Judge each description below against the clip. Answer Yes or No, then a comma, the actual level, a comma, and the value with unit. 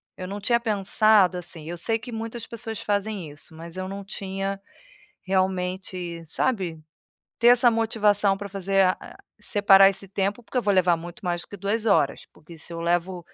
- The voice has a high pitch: Yes, high, 195 Hz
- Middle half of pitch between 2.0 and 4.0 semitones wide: Yes, average, 3.0 semitones